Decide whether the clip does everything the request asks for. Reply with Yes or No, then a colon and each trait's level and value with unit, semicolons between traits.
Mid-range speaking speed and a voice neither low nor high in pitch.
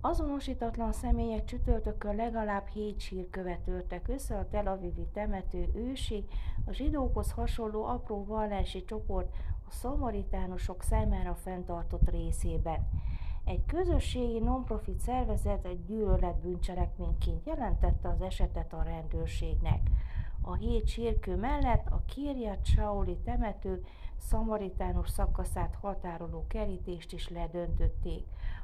No: slow, 100 wpm; medium, 170 Hz